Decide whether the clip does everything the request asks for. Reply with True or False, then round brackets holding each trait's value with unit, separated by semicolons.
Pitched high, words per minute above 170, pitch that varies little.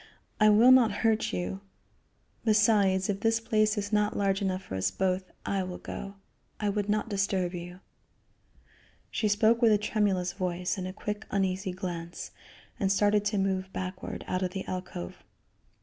False (195 Hz; 165 wpm; 2.2 semitones)